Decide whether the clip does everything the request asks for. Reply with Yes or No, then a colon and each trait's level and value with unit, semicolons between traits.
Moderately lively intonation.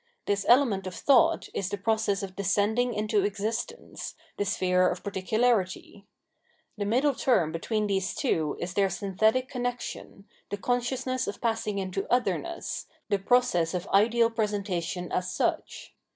Yes: average, 3.9 semitones